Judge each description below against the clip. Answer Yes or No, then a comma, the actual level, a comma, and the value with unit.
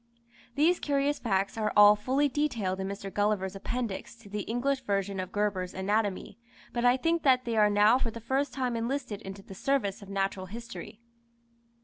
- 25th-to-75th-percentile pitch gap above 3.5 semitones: Yes, average, 4.4 semitones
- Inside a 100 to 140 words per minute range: No, average, 180 wpm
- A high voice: Yes, high, 215 Hz